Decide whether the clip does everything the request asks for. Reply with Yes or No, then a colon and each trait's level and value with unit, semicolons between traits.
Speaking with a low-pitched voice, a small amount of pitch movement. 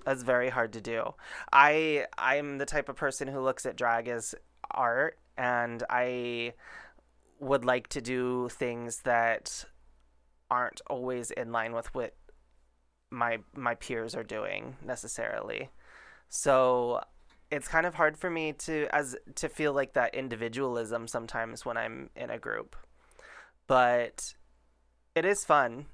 No: low, 125 Hz; average, 3.3 semitones